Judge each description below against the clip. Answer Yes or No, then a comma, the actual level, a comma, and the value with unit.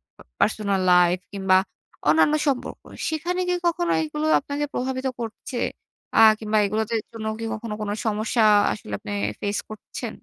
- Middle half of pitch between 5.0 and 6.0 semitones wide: Yes, wide, 5.5 semitones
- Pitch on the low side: No, high, 220 Hz